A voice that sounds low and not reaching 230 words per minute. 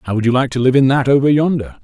No: low, 130 Hz; fast, 330 wpm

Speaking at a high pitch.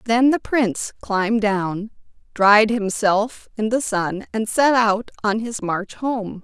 Yes: high, 215 Hz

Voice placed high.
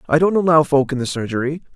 No: medium, 145 Hz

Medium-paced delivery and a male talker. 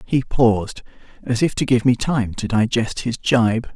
Yes: average, 175 wpm; male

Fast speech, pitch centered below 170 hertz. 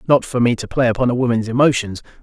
Yes: fast, 240 wpm; low, 120 Hz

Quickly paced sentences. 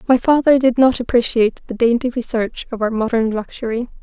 No: average, 180 wpm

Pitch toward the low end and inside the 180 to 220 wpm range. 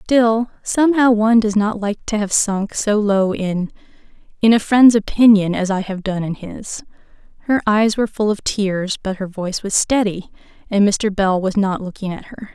No: high, 205 Hz; average, 190 wpm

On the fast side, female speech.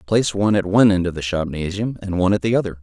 No: fast, 275 wpm; male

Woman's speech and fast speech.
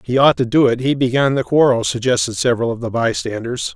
No: male; fast, 225 wpm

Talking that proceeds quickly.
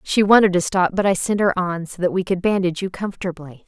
Yes: fast, 260 wpm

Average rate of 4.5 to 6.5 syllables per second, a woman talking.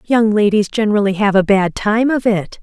Yes: 5.1 syllables/s; female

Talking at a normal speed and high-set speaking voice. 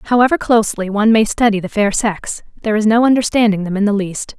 No: fast, 220 wpm; high, 215 Hz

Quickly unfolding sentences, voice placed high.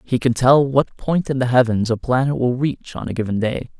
No: fast, 255 wpm; low, 125 Hz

